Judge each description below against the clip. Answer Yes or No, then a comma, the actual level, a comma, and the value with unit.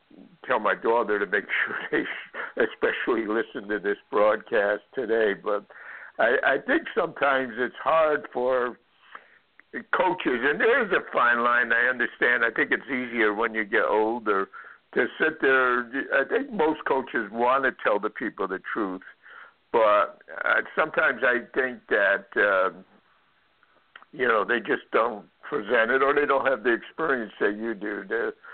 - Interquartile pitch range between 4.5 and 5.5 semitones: No, average, 3.9 semitones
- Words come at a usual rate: Yes, average, 160 wpm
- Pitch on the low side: Yes, low, 125 Hz